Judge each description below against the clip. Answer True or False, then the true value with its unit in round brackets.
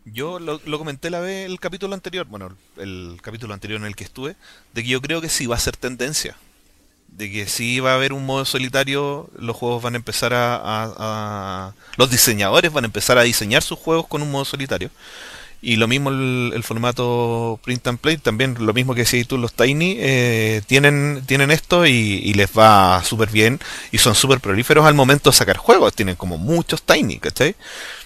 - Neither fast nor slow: False (210 wpm)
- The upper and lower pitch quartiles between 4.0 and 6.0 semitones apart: True (4.3 semitones)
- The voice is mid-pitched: False (125 Hz)